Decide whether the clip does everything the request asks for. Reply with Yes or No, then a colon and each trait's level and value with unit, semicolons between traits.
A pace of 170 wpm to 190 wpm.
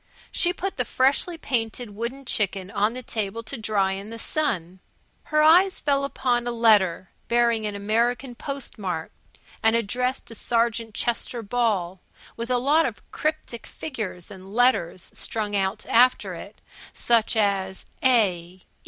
No: average, 145 wpm